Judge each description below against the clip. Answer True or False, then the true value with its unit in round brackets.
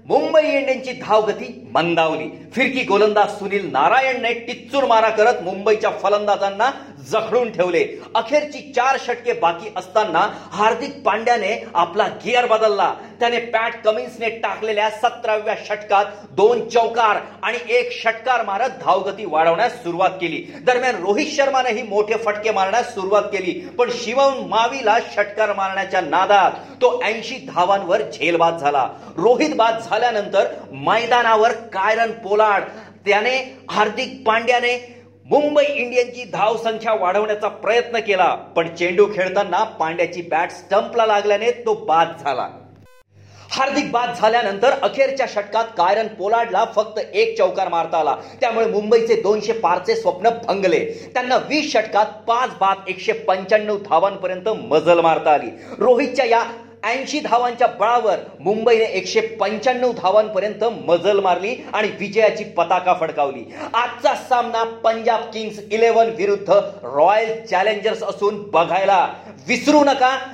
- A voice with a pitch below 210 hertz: False (220 Hz)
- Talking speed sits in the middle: True (120 wpm)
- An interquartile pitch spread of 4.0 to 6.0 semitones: False (3.4 semitones)